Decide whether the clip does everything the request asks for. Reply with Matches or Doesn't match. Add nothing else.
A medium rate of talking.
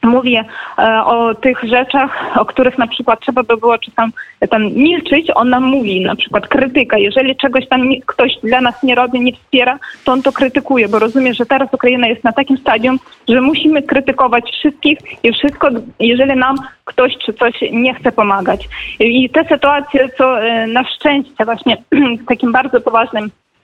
Doesn't match